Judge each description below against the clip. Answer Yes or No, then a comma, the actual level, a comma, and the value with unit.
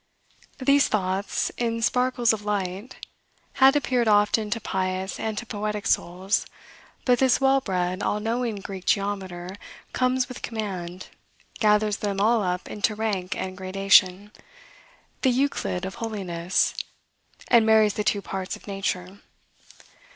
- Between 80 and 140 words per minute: Yes, slow, 135 wpm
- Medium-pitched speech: No, high, 205 Hz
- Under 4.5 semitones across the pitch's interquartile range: Yes, average, 3.4 semitones